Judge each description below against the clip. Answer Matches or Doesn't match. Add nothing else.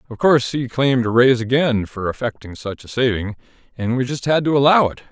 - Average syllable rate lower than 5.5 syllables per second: Doesn't match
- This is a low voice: Matches